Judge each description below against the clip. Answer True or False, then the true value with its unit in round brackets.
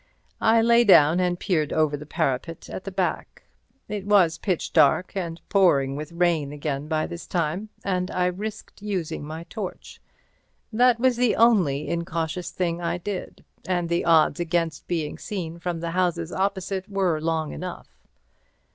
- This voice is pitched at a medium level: True (175 Hz)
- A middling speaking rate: True (160 wpm)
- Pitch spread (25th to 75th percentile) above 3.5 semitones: False (3.2 semitones)